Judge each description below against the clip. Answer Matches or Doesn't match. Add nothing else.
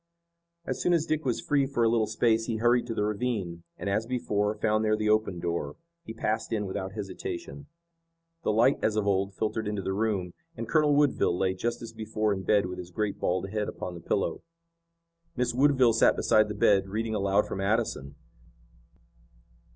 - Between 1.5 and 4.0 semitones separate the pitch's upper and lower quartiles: Matches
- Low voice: Matches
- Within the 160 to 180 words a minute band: Doesn't match